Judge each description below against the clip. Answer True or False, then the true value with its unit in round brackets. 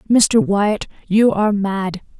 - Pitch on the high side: True (200 Hz)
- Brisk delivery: False (135 wpm)